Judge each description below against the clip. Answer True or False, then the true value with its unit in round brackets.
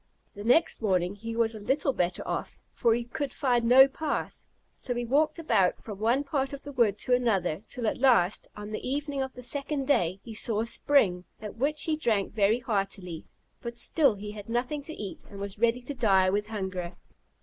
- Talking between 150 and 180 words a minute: False (205 wpm)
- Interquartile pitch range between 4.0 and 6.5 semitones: True (4.8 semitones)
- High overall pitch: True (230 Hz)